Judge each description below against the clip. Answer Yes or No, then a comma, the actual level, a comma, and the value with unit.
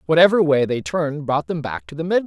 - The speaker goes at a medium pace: No, fast, 265 wpm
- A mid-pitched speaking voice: Yes, medium, 150 Hz